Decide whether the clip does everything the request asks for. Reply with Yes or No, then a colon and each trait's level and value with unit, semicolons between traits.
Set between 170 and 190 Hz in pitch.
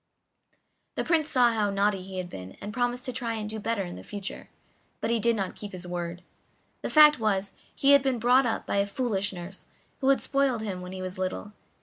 No: high, 210 Hz